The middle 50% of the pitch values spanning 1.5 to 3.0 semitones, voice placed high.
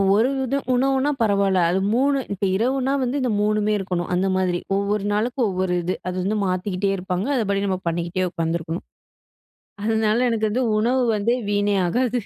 No: average, 4.3 semitones; high, 205 Hz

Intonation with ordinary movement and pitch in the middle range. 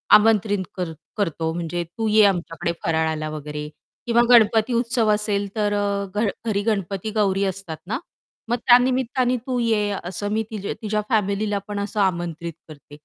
No: average, 4.1 semitones; high, 205 Hz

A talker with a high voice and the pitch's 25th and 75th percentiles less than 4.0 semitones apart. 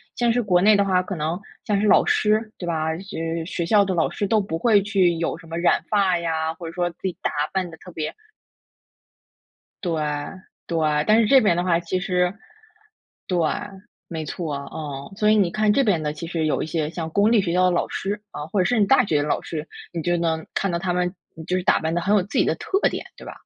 No: medium, 180 Hz; average, 3.6 semitones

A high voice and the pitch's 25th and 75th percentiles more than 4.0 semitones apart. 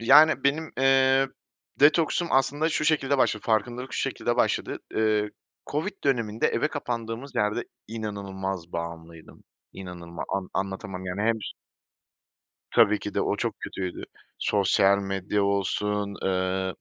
No: low, 105 Hz; wide, 5.6 semitones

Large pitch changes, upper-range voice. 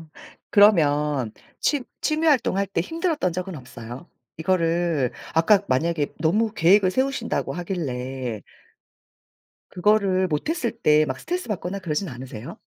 No: wide, 6.0 semitones; medium, 175 Hz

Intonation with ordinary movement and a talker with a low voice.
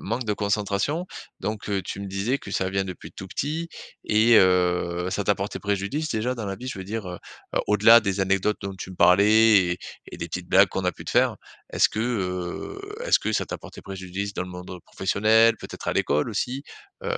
Yes: average, 3.1 semitones; low, 100 Hz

